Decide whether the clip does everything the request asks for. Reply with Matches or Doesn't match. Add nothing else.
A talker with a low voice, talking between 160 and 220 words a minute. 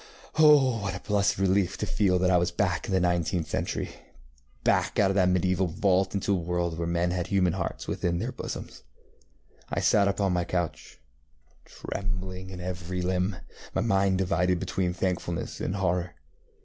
Matches